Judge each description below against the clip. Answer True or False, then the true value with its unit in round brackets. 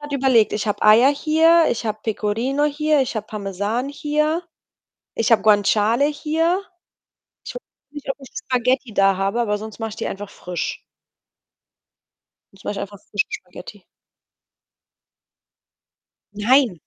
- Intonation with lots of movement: True (5.7 semitones)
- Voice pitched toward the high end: True (230 Hz)